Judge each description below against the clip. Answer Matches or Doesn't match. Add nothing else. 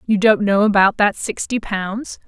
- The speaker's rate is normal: Matches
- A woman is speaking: Matches